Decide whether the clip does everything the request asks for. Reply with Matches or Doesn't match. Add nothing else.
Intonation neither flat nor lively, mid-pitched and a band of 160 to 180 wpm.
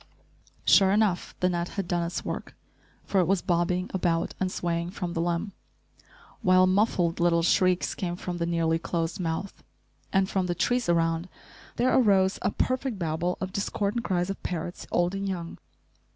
Doesn't match